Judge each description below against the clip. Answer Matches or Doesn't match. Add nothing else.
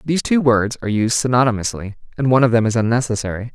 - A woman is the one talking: Doesn't match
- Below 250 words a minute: Matches